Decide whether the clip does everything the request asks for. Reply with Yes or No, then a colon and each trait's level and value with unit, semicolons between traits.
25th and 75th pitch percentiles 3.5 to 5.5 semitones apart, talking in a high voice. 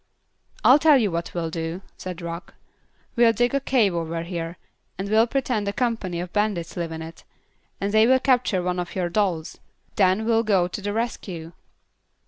Yes: average, 5.0 semitones; high, 195 Hz